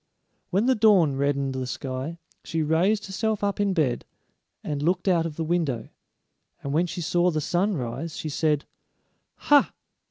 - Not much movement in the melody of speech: No, average, 5.0 semitones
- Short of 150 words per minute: No, average, 165 wpm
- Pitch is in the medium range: Yes, medium, 165 Hz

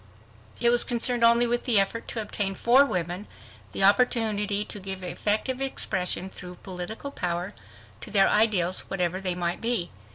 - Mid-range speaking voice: No, high, 205 Hz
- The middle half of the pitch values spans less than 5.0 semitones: Yes, average, 4.4 semitones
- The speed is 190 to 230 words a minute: No, average, 160 wpm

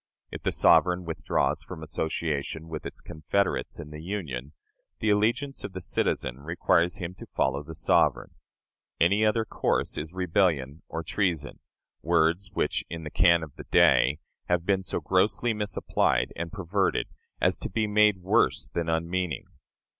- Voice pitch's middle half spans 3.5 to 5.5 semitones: Yes, average, 3.8 semitones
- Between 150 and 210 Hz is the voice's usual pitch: No, very low, 85 Hz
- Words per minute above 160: No, average, 155 wpm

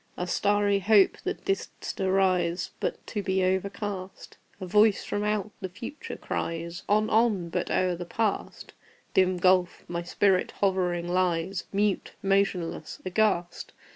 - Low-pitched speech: No, high, 190 Hz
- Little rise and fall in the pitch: Yes, narrow, 2.3 semitones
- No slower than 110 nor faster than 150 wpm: Yes, average, 140 wpm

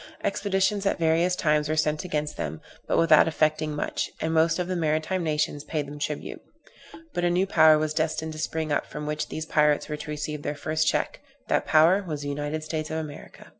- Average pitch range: No, narrow, 1.4 semitones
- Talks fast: Yes, fast, 210 wpm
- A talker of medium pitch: Yes, medium, 155 Hz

